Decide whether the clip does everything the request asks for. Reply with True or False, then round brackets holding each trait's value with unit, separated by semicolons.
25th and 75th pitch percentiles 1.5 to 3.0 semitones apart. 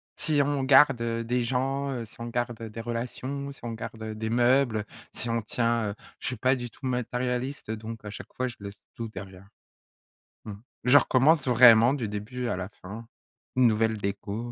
True (2.6 semitones)